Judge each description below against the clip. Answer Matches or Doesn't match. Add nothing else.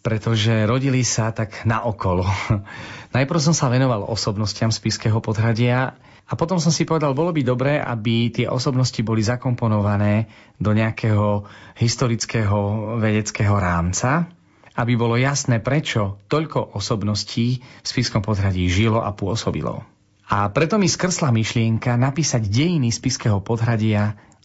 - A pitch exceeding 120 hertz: Doesn't match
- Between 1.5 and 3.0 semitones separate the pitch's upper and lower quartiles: Doesn't match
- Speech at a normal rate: Matches